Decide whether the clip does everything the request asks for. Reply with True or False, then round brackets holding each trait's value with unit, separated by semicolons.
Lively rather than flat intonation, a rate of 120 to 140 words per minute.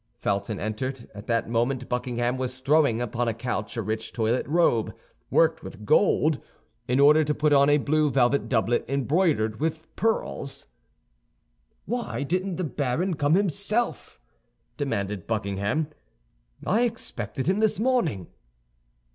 True (5.7 semitones; 135 wpm)